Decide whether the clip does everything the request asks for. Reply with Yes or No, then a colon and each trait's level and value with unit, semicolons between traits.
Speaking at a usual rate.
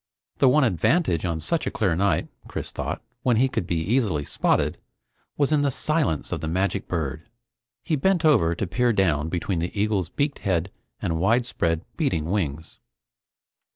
Yes: average, 170 wpm